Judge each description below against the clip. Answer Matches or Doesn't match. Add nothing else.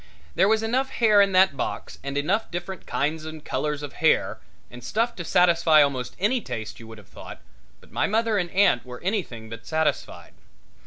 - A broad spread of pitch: Matches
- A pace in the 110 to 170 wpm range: Doesn't match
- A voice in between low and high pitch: Matches